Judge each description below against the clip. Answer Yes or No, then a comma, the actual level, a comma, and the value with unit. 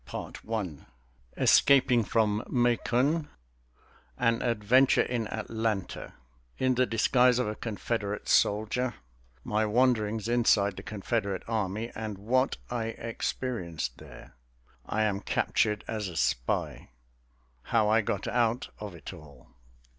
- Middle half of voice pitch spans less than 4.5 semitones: Yes, average, 2.7 semitones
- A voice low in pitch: Yes, low, 110 Hz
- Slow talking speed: Yes, slow, 120 wpm